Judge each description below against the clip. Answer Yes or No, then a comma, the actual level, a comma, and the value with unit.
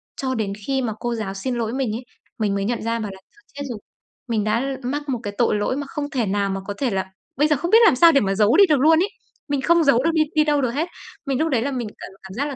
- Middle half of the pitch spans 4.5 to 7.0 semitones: Yes, average, 5.1 semitones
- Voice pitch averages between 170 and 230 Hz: No, very high, 255 Hz